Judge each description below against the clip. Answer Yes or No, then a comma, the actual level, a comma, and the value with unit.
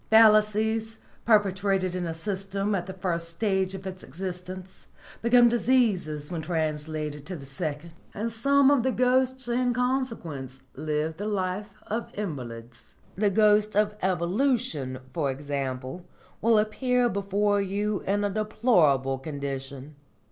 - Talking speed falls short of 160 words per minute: Yes, slow, 135 wpm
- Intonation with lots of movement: Yes, wide, 5.9 semitones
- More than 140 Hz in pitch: Yes, high, 190 Hz